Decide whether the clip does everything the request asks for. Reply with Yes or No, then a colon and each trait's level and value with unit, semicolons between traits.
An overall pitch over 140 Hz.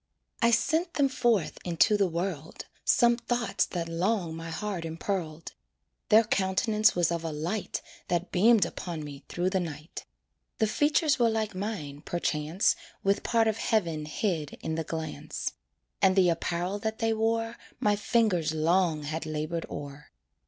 Yes: medium, 185 Hz